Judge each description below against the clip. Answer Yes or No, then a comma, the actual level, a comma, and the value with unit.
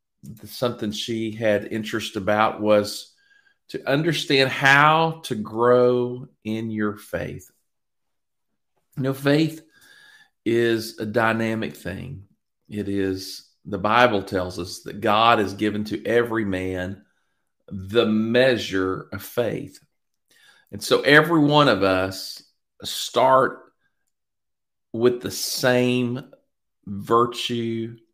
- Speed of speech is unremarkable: No, slow, 105 wpm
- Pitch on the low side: Yes, low, 115 Hz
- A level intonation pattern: No, average, 3.2 semitones